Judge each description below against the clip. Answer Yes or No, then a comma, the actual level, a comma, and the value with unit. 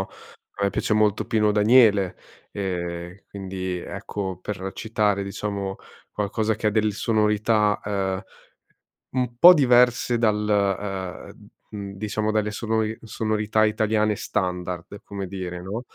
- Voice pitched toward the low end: Yes, low, 105 Hz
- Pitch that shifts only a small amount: Yes, narrow, 2.0 semitones